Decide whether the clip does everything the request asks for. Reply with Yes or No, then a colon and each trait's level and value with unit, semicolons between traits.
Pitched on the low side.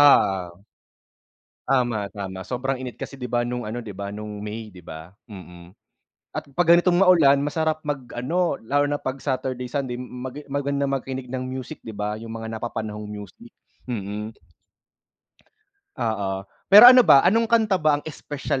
Yes: low, 125 Hz